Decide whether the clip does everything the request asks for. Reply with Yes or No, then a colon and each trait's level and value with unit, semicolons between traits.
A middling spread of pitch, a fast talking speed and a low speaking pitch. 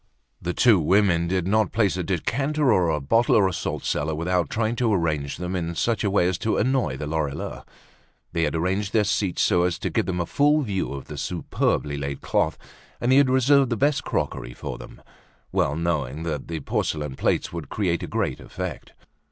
No: wide, 5.7 semitones; fast, 210 wpm; very low, 90 Hz